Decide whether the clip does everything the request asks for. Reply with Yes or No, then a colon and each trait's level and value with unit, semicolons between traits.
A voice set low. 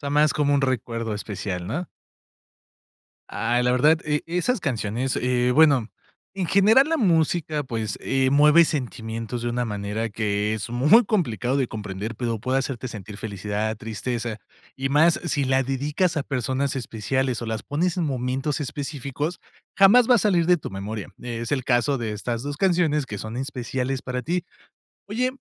Yes: low, 130 Hz